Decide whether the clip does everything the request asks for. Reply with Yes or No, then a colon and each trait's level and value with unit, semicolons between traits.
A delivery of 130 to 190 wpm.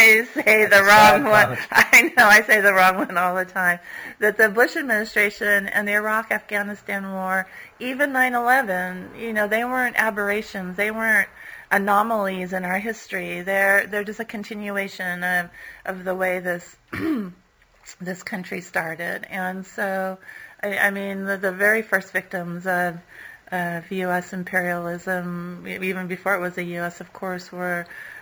Yes: average, 155 wpm